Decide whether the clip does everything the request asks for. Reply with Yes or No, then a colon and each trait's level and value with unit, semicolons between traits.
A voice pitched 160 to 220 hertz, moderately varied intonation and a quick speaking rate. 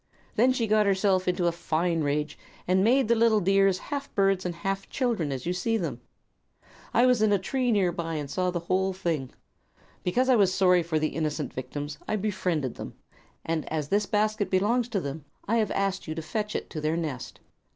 Yes: medium, 185 Hz; average, 4.8 semitones; fast, 210 wpm